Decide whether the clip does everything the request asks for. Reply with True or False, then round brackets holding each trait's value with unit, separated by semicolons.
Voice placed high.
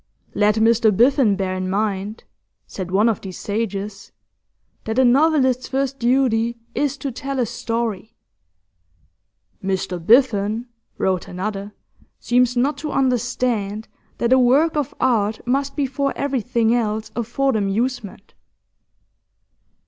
True (235 Hz)